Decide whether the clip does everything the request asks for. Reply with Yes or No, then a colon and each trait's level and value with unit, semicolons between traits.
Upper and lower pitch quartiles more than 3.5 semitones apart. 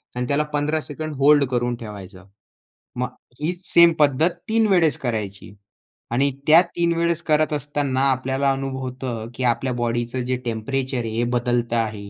Yes: average, 4.1 semitones